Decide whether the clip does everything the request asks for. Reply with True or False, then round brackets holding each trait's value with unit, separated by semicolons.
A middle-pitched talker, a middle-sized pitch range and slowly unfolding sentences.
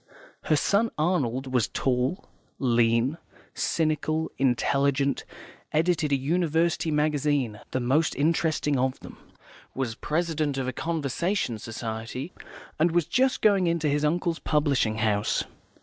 True (150 Hz; 4.2 semitones; 120 wpm)